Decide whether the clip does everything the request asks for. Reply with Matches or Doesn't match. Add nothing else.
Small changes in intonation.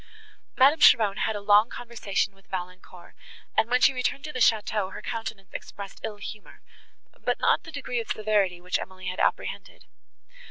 Doesn't match